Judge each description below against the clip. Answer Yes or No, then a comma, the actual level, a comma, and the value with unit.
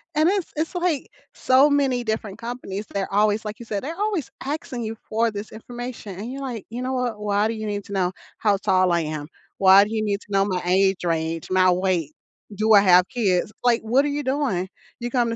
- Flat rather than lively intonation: No, average, 4.5 semitones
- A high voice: Yes, high, 215 Hz